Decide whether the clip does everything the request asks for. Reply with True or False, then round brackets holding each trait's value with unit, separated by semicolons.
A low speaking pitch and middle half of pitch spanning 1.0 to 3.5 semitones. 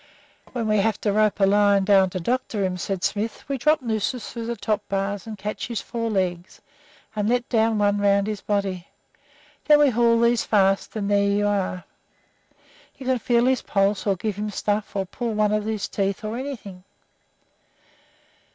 False (210 Hz; 2.6 semitones)